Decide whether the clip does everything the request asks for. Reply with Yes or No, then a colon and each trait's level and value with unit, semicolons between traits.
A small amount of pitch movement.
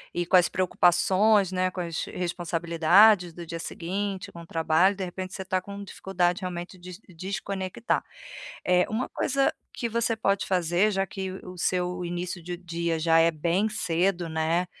Yes: narrow, 2.0 semitones